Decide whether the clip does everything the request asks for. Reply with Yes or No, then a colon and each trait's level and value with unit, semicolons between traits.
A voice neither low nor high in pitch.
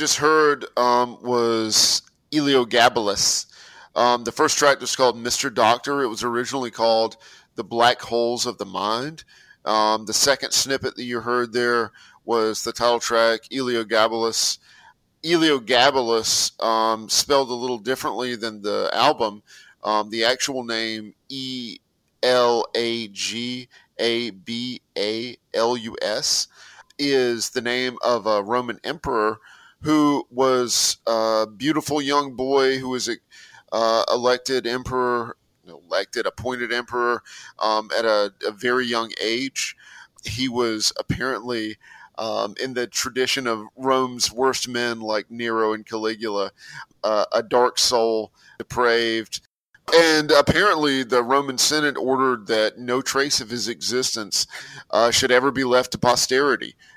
No: low, 120 Hz